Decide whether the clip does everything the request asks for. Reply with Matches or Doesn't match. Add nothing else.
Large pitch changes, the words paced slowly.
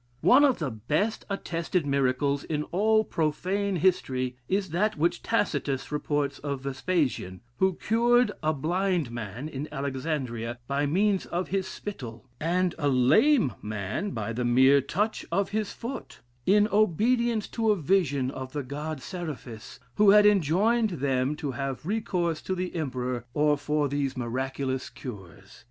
Doesn't match